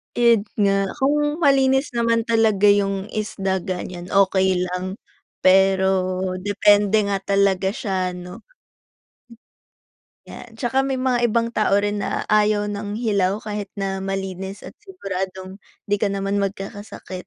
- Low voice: No, high, 200 Hz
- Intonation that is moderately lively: No, narrow, 2.3 semitones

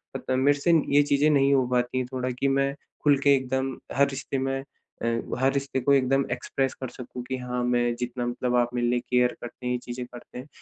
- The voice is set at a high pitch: No, low, 130 Hz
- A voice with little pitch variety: Yes, narrow, 1.8 semitones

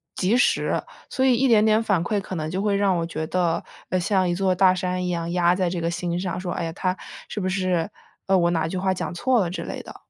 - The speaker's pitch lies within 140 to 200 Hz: Yes, medium, 185 Hz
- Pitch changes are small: Yes, narrow, 2.2 semitones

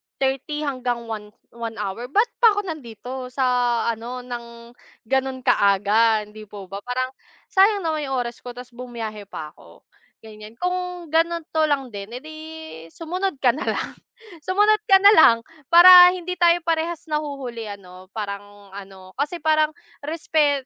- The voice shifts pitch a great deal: Yes, wide, 6.6 semitones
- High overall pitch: Yes, very high, 255 Hz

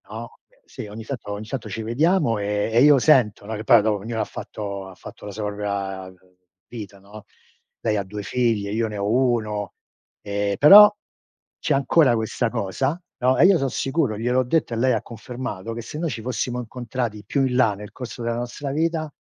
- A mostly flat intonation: No, average, 3.9 semitones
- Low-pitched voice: Yes, low, 115 Hz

